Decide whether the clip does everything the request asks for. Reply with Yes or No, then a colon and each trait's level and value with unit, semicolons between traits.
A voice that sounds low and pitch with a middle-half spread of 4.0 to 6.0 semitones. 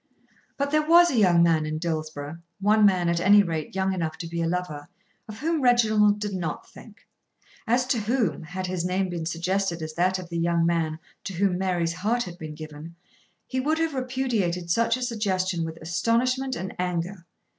No: medium, 185 Hz; average, 5.1 semitones